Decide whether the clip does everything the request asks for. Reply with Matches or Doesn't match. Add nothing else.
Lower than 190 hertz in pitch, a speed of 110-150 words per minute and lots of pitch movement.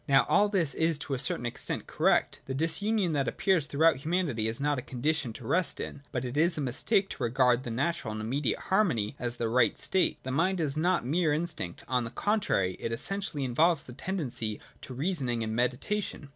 Doesn't match